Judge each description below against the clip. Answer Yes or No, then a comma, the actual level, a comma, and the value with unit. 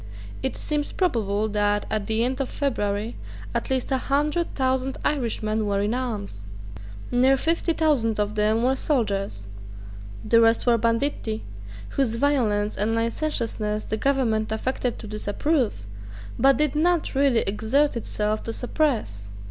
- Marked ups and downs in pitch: No, average, 4.3 semitones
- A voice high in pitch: Yes, high, 230 Hz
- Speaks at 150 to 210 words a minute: No, average, 140 wpm